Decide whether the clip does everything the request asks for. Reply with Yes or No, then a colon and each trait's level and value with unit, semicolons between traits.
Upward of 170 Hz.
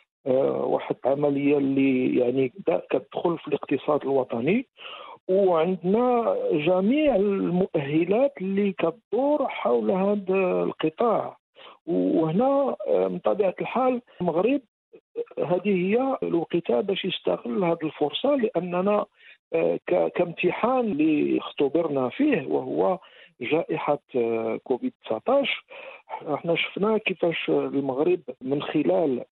Yes: medium, 185 Hz